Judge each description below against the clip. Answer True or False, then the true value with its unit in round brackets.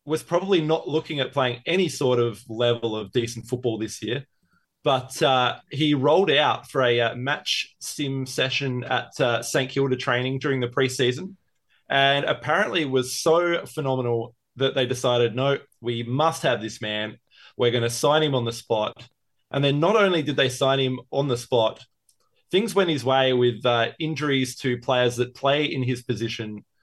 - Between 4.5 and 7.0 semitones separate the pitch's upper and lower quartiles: False (3.3 semitones)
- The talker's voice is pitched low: True (130 Hz)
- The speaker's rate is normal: True (180 wpm)